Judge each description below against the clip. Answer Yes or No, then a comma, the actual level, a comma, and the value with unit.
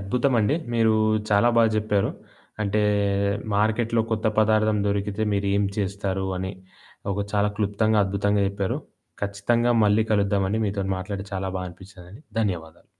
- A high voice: No, low, 100 Hz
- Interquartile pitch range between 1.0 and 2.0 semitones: Yes, narrow, 1.7 semitones